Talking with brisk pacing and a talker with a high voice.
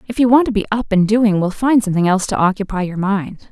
Yes: fast, 275 wpm; high, 205 Hz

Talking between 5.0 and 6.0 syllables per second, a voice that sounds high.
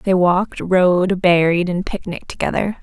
No: 5.1 syllables/s; medium, 180 Hz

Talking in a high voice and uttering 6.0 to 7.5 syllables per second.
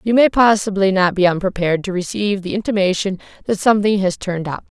Yes: high, 195 Hz; 6.5 syllables/s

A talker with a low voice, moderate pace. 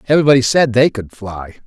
Yes: low, 120 Hz; average, 180 wpm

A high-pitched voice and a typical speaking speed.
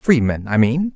No: low, 135 Hz; average, 190 wpm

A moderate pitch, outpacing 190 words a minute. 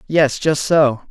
No: medium, 145 Hz; average, 165 wpm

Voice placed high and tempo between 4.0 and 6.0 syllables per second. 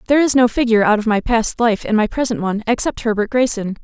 No: high, 230 Hz; 6.7 syllables/s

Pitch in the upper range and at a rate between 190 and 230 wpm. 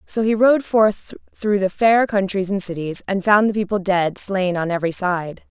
Yes: high, 195 Hz; fast, 205 wpm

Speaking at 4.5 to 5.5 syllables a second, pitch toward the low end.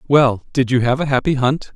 Yes: 5.3 syllables/s; low, 130 Hz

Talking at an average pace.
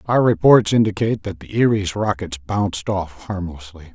Yes: average, 150 wpm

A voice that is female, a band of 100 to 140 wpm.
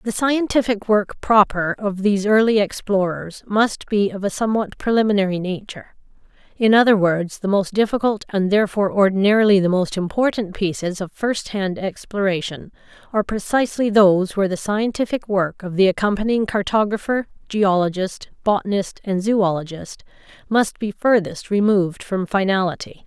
Yes: female; slow, 135 wpm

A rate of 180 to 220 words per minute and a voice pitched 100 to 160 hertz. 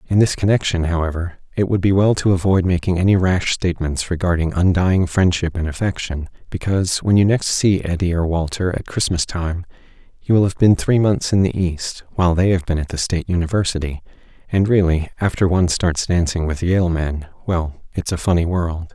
No: average, 190 wpm; very low, 90 Hz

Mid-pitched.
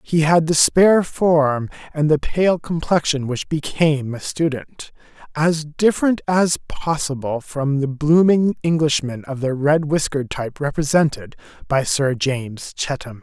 Yes: medium, 150 Hz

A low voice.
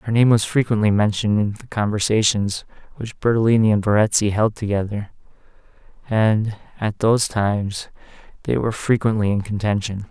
Yes: low, 105 Hz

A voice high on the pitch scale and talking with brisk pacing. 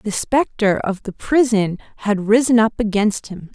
No: high, 215 Hz; average, 170 wpm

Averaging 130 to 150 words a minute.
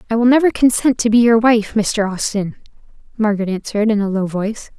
No: average, 200 wpm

